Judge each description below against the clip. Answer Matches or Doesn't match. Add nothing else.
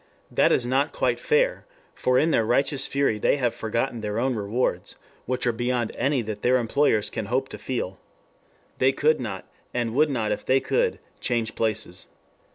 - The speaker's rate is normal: Matches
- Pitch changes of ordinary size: Matches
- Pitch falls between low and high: Doesn't match